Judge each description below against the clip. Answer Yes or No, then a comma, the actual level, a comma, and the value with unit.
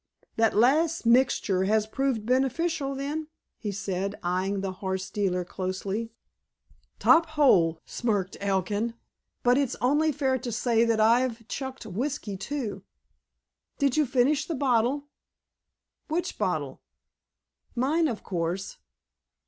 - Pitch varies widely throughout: Yes, wide, 5.7 semitones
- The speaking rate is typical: No, slow, 120 wpm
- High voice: Yes, high, 235 Hz